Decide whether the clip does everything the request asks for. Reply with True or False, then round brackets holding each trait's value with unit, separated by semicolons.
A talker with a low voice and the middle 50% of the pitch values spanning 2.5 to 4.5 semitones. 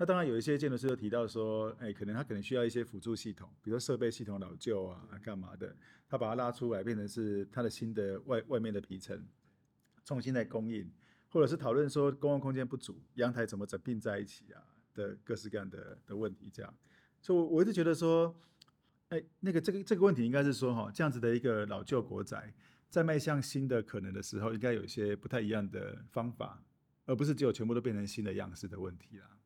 False (120 Hz; 5.2 semitones)